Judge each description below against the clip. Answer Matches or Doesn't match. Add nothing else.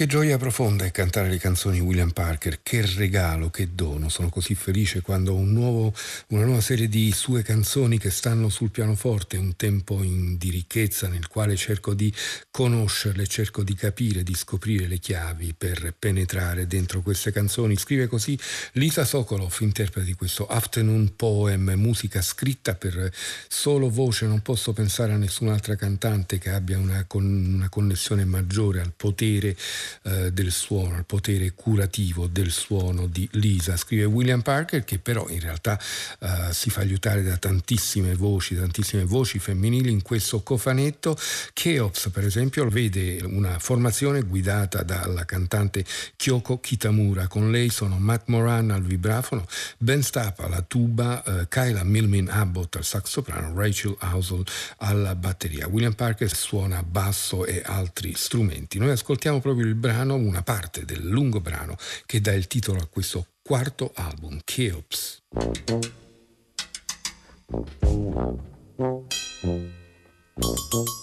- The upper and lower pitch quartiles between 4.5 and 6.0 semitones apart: Doesn't match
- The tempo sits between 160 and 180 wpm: Doesn't match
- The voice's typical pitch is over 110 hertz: Doesn't match